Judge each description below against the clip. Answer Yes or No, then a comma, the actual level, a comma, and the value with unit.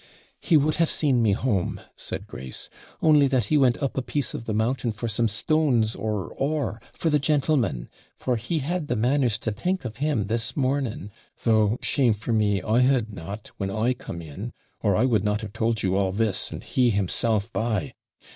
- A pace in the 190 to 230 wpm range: Yes, average, 200 wpm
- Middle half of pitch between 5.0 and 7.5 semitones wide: No, average, 4.5 semitones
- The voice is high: No, low, 115 Hz